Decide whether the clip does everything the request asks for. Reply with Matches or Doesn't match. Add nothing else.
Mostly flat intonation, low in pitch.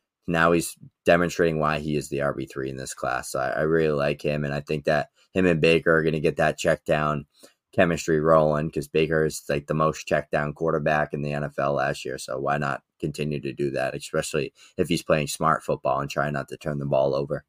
Matches